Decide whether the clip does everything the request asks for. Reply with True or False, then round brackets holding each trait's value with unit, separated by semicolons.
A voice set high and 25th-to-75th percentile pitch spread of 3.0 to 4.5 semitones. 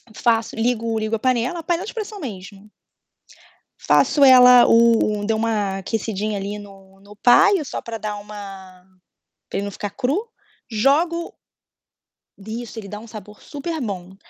True (220 Hz; 3.6 semitones)